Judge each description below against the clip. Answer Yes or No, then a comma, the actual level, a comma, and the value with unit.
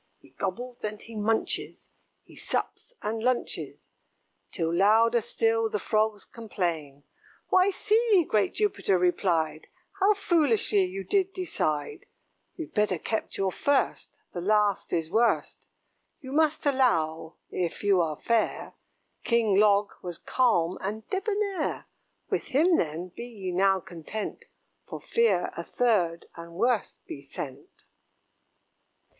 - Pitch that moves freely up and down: Yes, wide, 6.4 semitones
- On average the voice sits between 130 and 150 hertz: No, high, 215 Hz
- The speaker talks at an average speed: No, slow, 125 wpm